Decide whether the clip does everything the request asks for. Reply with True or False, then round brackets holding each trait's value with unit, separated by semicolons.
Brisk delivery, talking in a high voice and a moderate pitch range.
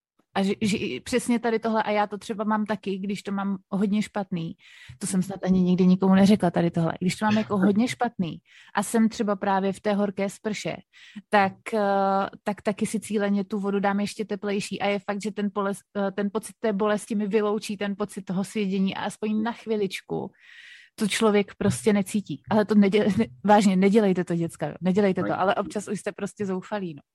False (200 wpm; 205 Hz; 1.6 semitones)